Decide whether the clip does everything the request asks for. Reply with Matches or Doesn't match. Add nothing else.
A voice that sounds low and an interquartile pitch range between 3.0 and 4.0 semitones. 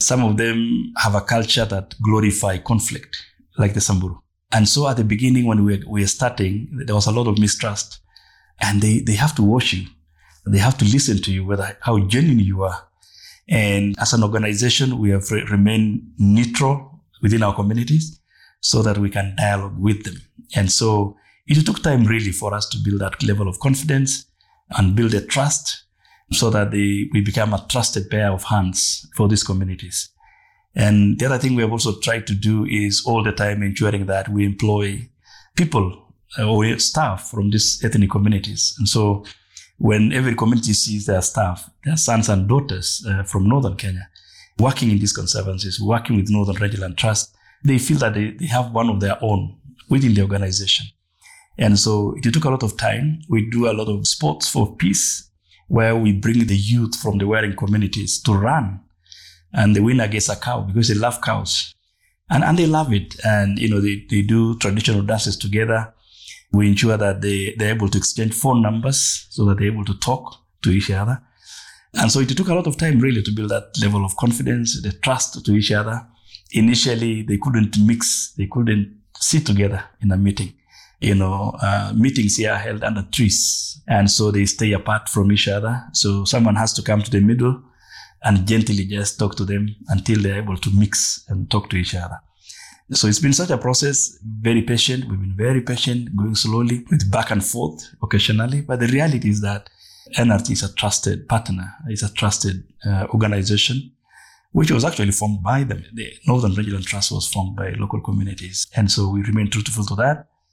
Doesn't match